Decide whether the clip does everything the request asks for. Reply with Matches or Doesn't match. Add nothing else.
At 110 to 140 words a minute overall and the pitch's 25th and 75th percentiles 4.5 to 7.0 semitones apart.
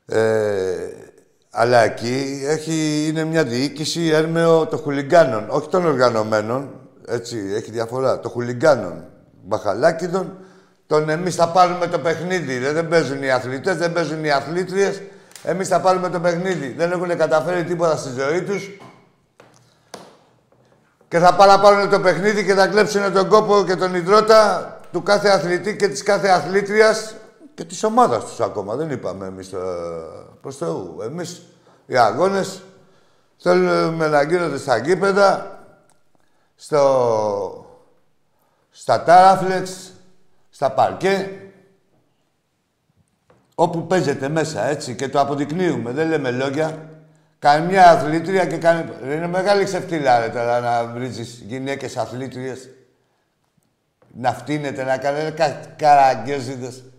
Matches